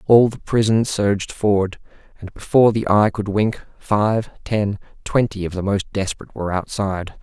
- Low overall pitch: Yes, low, 105 Hz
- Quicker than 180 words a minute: No, average, 165 wpm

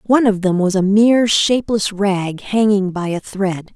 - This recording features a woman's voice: Yes, female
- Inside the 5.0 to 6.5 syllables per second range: No, 4.7 syllables/s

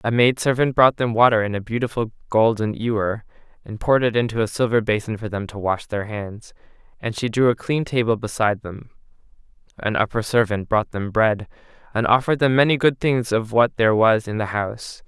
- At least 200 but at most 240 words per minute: Yes, fast, 205 wpm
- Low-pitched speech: Yes, low, 115 Hz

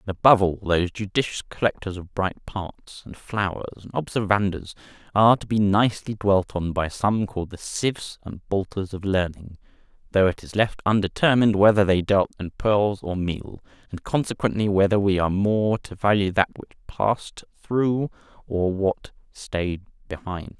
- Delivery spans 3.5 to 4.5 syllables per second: No, 5.0 syllables/s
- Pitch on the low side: Yes, low, 100 Hz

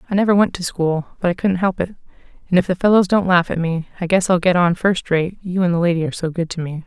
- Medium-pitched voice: Yes, medium, 180 Hz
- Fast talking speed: Yes, fast, 295 wpm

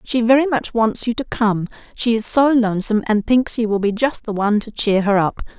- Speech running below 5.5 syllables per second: No, 5.6 syllables/s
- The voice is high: Yes, high, 225 Hz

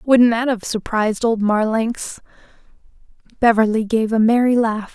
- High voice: Yes, high, 225 Hz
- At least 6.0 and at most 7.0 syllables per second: No, 4.6 syllables/s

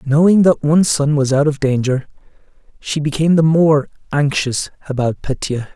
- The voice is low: No, medium, 145 Hz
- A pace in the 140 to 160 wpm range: Yes, average, 155 wpm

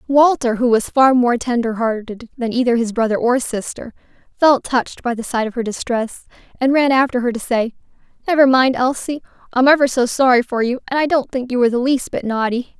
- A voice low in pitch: No, very high, 250 Hz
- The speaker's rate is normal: No, fast, 220 wpm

